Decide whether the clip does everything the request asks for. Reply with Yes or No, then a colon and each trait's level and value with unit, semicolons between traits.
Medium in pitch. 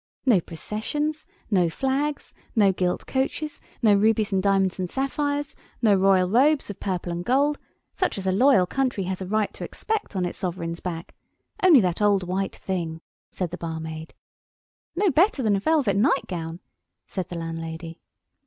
No: high, 195 Hz